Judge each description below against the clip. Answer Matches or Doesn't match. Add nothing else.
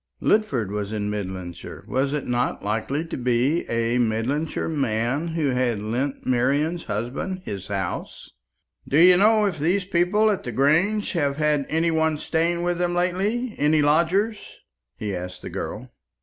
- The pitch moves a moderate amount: Doesn't match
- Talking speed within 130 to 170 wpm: Matches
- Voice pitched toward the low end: Doesn't match